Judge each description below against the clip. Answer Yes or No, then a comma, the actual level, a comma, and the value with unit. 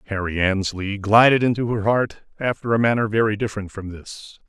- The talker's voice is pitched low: Yes, low, 105 Hz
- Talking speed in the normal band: Yes, average, 175 wpm